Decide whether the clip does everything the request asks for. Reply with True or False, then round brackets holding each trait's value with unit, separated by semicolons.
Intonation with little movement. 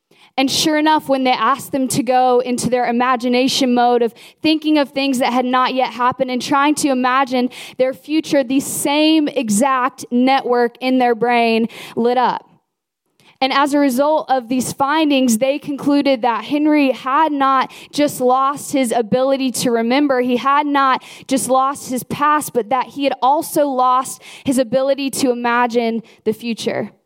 True (2.1 semitones)